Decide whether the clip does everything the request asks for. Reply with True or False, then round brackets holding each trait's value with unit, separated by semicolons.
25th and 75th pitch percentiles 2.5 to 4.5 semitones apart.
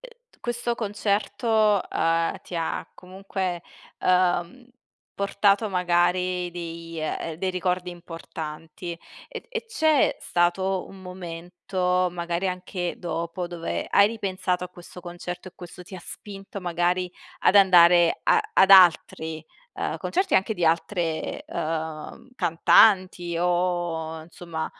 False (2.1 semitones)